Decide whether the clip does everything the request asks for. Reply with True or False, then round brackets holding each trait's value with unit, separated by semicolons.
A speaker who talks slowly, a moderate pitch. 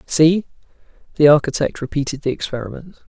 True (115 wpm; 150 Hz)